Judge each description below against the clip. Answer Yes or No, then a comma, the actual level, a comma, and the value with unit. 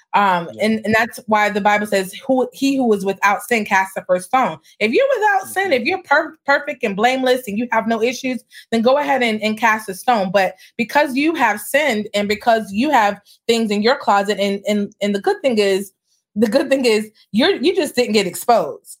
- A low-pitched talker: No, high, 230 Hz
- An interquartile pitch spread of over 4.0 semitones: Yes, average, 4.7 semitones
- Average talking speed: No, fast, 225 wpm